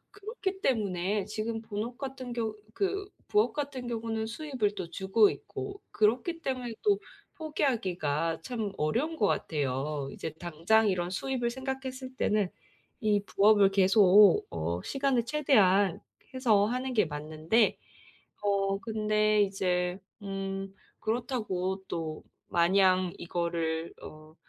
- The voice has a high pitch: Yes, high, 210 Hz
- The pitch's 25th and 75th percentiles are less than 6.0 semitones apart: Yes, average, 5.3 semitones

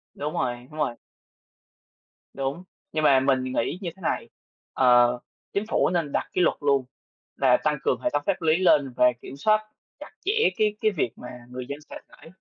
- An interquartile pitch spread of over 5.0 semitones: Yes, wide, 5.6 semitones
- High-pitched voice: No, medium, 145 Hz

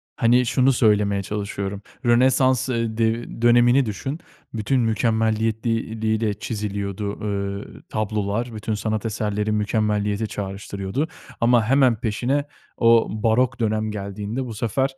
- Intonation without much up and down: Yes, narrow, 2.3 semitones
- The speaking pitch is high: No, low, 110 Hz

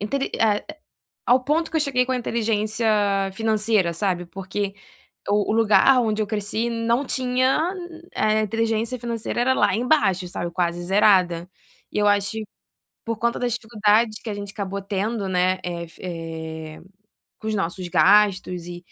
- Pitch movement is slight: No, average, 3.8 semitones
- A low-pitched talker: No, high, 210 Hz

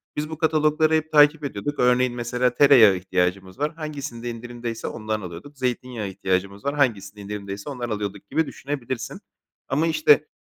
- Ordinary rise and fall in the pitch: No, wide, 6.2 semitones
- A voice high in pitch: No, low, 125 Hz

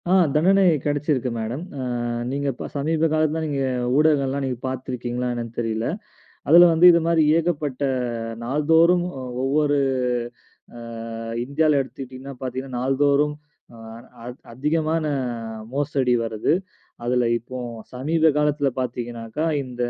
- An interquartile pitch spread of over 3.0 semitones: Yes, average, 3.6 semitones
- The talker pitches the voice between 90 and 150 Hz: Yes, medium, 140 Hz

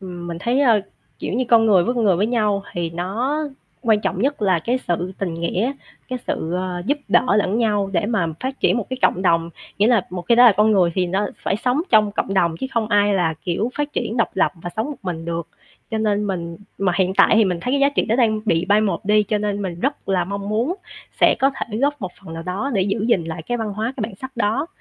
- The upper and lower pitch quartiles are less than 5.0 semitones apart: Yes, average, 4.4 semitones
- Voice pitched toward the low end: No, high, 205 Hz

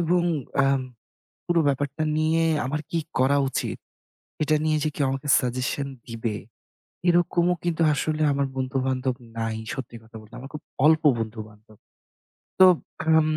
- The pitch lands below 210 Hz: Yes, medium, 140 Hz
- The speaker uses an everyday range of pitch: Yes, average, 3.8 semitones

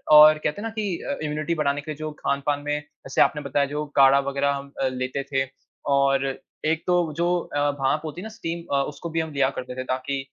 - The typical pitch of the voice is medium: Yes, medium, 145 Hz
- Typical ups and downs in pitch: No, narrow, 2.3 semitones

